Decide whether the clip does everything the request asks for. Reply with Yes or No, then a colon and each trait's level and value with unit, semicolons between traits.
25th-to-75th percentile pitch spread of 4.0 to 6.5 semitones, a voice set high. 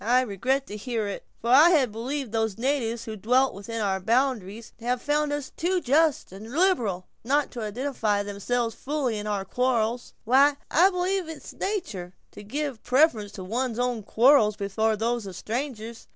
Yes: average, 4.6 semitones; high, 240 Hz